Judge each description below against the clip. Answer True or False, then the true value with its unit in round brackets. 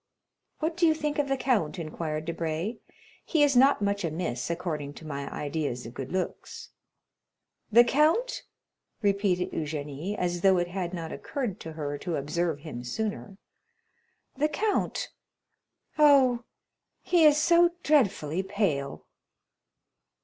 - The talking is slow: True (130 wpm)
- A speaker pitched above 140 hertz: True (185 Hz)